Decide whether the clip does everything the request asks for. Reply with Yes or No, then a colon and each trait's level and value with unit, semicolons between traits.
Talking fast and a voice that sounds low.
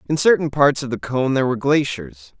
Yes: fast, 225 wpm; low, 130 Hz